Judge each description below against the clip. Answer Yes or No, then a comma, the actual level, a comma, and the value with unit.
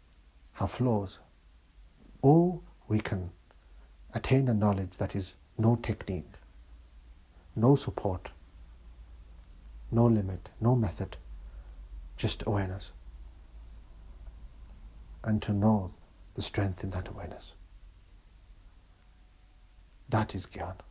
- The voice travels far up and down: Yes, wide, 6.1 semitones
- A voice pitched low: Yes, very low, 90 Hz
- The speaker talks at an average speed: No, slow, 90 wpm